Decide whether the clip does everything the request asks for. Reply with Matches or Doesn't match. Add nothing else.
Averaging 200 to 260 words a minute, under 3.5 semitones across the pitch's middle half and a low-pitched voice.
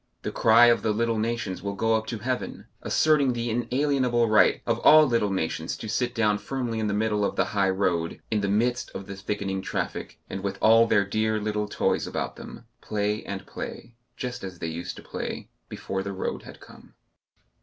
Matches